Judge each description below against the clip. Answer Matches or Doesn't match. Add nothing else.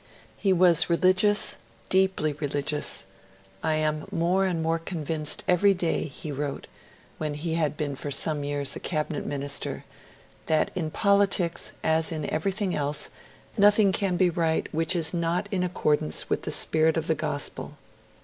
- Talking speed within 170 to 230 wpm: Doesn't match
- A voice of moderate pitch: Matches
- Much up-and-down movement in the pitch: Doesn't match